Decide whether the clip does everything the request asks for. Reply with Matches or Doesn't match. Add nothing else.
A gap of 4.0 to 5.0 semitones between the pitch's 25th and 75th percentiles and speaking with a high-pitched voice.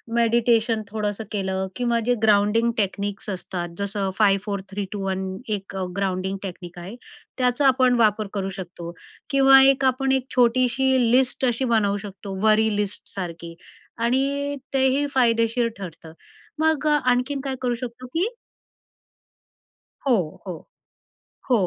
Matches